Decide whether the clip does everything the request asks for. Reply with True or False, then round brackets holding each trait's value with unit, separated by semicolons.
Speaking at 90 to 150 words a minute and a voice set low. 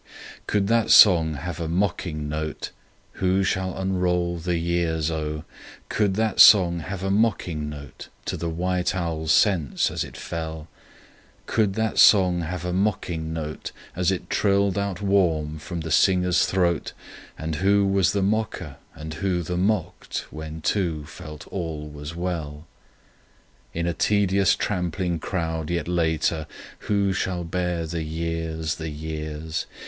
True (145 wpm; 85 Hz)